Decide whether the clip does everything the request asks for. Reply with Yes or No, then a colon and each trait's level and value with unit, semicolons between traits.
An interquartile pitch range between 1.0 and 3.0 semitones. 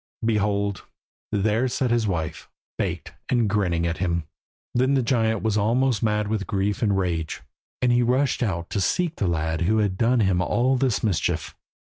No: average, 4.2 semitones